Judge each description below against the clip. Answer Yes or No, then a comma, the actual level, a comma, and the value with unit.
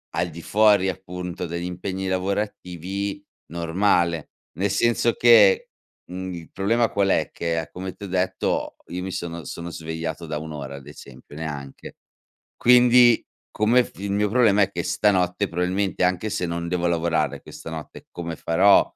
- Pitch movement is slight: No, average, 3.2 semitones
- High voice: No, very low, 90 Hz